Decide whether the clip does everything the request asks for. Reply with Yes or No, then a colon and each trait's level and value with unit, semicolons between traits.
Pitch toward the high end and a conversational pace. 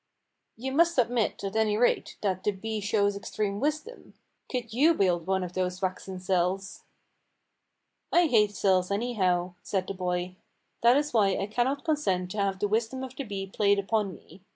Yes: high, 205 Hz; average, 175 wpm